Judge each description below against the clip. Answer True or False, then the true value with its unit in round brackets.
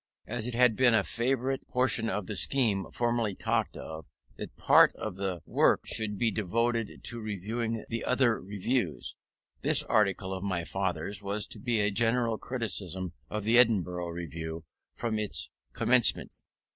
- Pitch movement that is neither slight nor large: True (3.7 semitones)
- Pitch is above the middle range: False (110 Hz)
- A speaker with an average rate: True (160 wpm)